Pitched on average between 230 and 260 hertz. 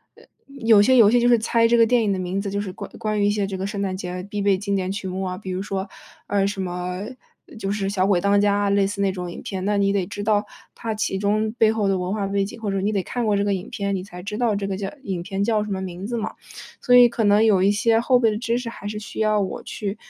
No: high, 200 Hz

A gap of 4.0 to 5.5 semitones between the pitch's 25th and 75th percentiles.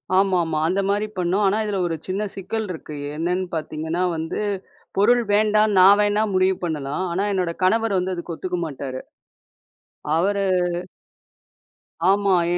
No: average, 3.3 semitones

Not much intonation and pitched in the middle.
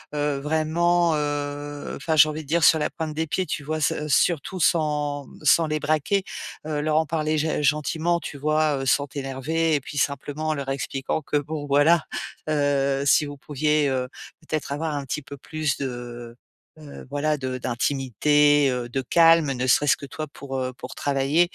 Yes: narrow, 2.1 semitones; medium, 150 Hz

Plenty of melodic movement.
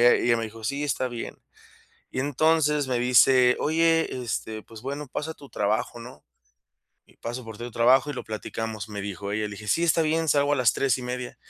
No: average, 4.5 semitones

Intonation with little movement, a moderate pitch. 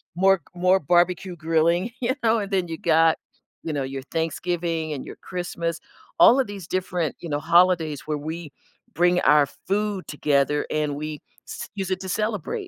No: average, 3.3 semitones; medium, 170 Hz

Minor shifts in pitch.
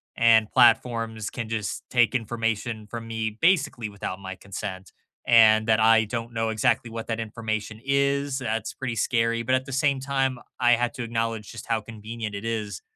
Yes: narrow, 1.9 semitones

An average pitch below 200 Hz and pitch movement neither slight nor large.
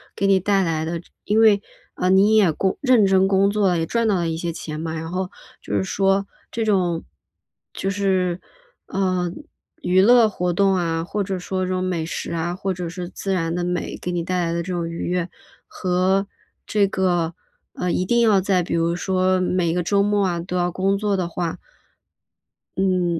No: medium, 185 Hz; narrow, 2.2 semitones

